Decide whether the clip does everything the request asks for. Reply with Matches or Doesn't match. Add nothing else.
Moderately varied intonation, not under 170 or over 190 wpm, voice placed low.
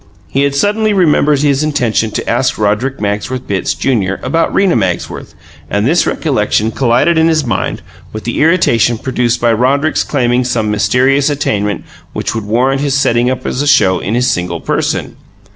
Matches